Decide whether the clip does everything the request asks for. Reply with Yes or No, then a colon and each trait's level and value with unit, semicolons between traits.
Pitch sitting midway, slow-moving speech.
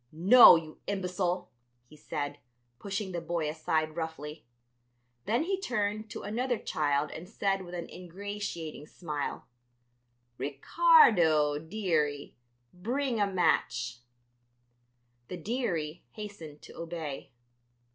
Yes: medium, 175 Hz; slow, 105 wpm